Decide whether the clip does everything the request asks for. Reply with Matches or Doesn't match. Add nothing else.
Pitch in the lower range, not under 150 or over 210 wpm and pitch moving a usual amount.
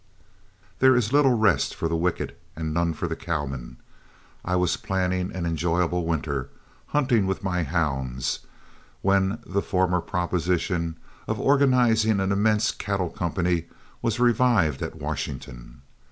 Doesn't match